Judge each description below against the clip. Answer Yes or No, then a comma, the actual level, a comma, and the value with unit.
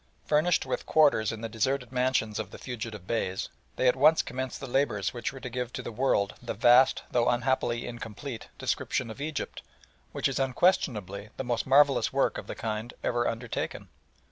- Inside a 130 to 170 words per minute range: No, average, 185 wpm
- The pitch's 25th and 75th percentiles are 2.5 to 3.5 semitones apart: Yes, average, 3.1 semitones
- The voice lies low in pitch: Yes, low, 125 Hz